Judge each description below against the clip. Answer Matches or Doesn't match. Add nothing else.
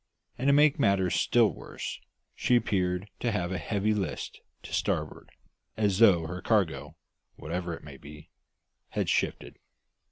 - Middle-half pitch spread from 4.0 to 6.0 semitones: Matches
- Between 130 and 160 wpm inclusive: Matches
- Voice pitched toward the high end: Doesn't match